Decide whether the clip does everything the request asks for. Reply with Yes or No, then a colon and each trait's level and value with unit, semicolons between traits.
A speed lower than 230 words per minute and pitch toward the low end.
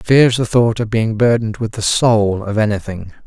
Yes: average, 200 wpm; low, 110 Hz